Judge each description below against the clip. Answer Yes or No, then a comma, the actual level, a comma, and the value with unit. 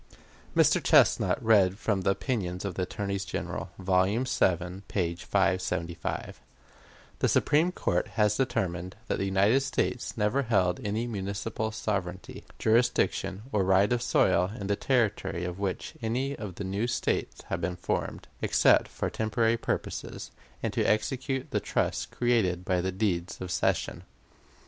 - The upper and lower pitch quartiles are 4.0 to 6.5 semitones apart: No, average, 3.6 semitones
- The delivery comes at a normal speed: Yes, average, 150 wpm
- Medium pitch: No, low, 100 Hz